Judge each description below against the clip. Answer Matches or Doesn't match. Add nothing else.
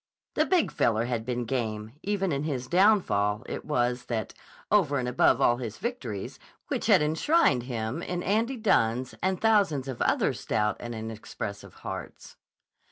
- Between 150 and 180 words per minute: Matches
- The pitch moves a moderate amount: Doesn't match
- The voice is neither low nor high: Doesn't match